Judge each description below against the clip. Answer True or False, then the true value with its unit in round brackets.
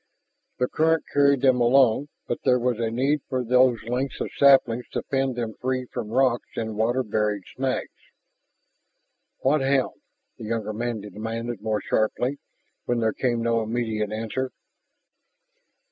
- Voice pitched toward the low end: True (120 Hz)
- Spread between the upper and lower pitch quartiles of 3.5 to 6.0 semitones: False (2.8 semitones)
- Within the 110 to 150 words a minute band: True (145 wpm)